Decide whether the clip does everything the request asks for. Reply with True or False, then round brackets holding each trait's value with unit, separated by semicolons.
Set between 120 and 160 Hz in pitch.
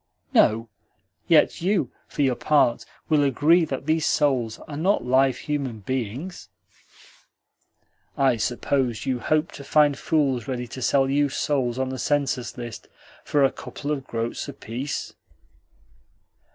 True (135 Hz)